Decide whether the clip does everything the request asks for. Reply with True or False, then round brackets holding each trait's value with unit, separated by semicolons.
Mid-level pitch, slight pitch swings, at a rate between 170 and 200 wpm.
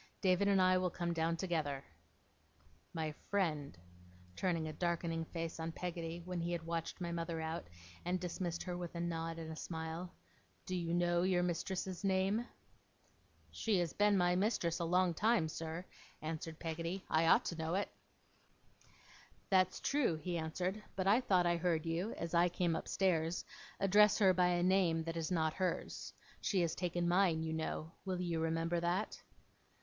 True (175 Hz; 2.0 semitones; 175 wpm)